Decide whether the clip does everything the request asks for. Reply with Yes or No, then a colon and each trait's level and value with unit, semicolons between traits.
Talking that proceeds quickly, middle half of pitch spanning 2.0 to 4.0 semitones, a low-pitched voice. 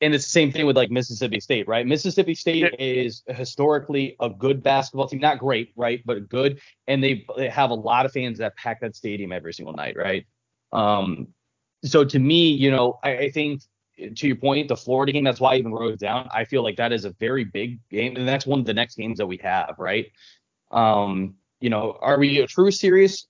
Yes: fast, 225 wpm; average, 3.7 semitones; low, 130 Hz